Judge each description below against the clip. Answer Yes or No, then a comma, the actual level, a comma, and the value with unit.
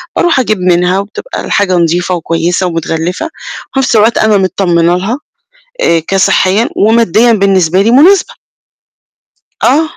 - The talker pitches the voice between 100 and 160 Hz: No, high, 195 Hz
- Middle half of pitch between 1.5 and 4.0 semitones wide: No, average, 4.6 semitones